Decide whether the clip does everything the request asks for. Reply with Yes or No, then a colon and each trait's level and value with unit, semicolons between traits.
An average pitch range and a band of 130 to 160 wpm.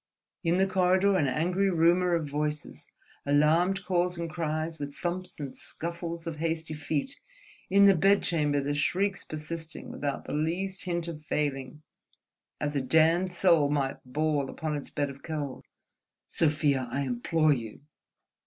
Yes: average, 3.3 semitones; average, 150 wpm